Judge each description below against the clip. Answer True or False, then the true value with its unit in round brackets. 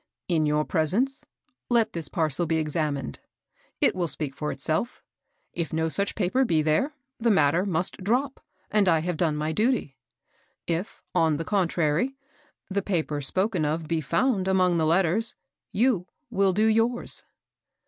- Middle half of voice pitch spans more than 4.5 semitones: True (4.9 semitones)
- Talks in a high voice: False (175 Hz)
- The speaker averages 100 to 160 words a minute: True (155 wpm)